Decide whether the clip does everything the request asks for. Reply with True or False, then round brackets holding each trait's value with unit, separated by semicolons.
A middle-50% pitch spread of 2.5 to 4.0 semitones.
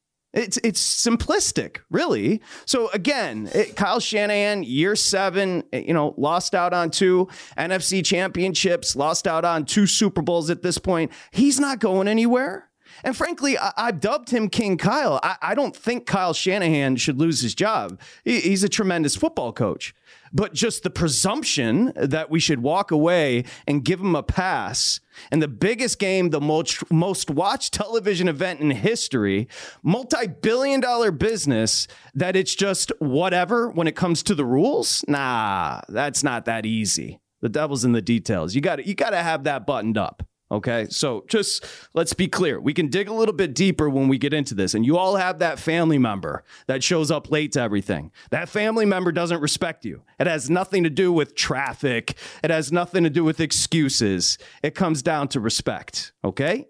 False (5.4 semitones)